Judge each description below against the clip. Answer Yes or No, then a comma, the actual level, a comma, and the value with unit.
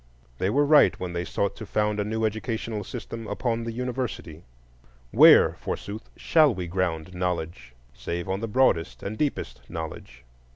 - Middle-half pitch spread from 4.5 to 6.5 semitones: Yes, average, 4.9 semitones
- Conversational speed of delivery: Yes, average, 160 wpm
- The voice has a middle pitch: No, low, 100 Hz